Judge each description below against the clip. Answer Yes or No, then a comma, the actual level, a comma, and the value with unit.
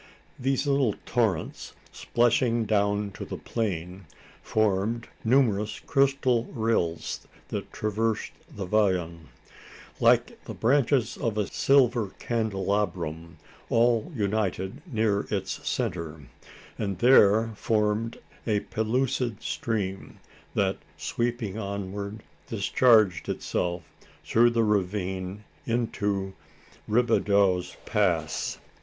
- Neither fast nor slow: No, slow, 95 wpm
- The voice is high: No, low, 105 Hz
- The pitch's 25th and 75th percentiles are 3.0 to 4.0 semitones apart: Yes, average, 3.3 semitones